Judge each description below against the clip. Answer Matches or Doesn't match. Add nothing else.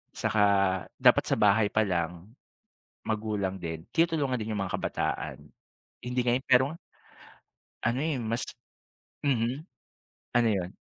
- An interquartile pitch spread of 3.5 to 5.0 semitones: Matches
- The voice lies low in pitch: Matches